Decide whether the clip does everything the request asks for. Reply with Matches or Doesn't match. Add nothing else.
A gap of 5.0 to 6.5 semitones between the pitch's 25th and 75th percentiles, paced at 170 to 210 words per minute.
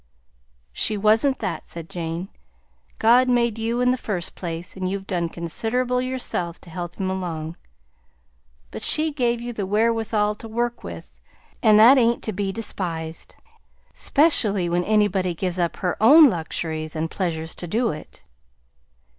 Doesn't match